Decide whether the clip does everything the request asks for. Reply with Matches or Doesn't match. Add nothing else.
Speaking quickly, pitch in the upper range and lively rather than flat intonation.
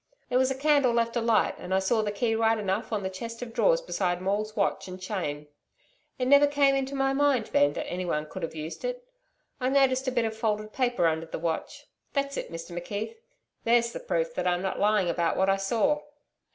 Matches